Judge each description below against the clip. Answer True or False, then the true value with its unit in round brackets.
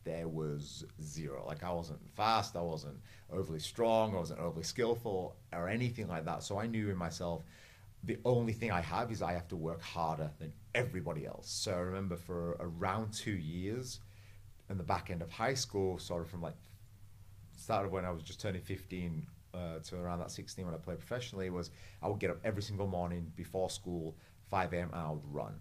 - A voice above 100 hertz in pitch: False (90 Hz)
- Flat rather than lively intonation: False (3.4 semitones)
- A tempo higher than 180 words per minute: True (205 wpm)